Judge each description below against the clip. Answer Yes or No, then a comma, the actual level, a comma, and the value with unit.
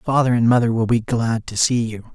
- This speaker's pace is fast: Yes, fast, 250 wpm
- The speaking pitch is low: Yes, low, 115 Hz